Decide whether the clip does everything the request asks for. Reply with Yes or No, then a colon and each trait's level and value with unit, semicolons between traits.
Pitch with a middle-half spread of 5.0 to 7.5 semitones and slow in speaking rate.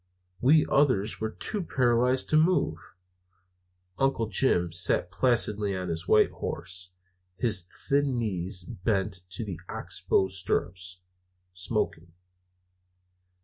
Yes: wide, 5.5 semitones; slow, 110 wpm